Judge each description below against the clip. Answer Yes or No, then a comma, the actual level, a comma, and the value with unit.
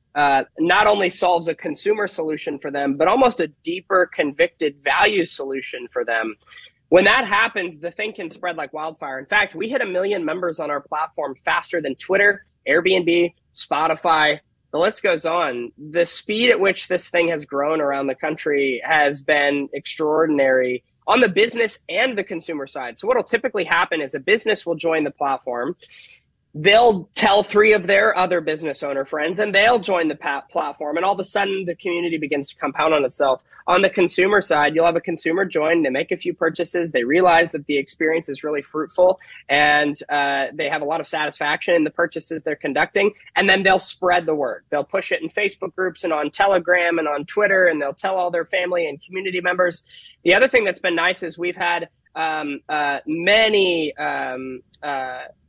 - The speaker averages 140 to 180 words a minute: No, average, 195 wpm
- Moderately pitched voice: Yes, medium, 170 Hz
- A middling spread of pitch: Yes, average, 4.3 semitones